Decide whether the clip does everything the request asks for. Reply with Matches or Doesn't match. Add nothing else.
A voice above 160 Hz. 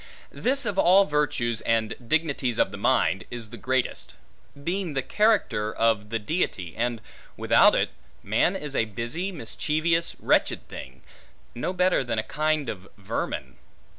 Doesn't match